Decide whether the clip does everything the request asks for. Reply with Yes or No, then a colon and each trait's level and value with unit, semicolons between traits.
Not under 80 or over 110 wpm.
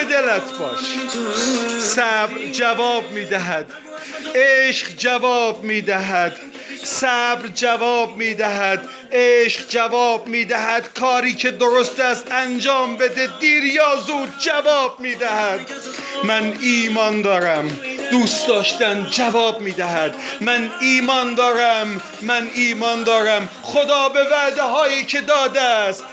Yes: slow, 105 wpm